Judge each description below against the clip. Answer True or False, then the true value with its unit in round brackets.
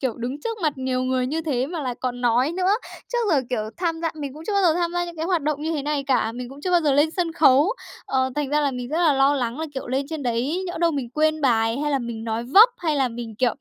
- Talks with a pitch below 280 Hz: False (285 Hz)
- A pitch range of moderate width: True (4.3 semitones)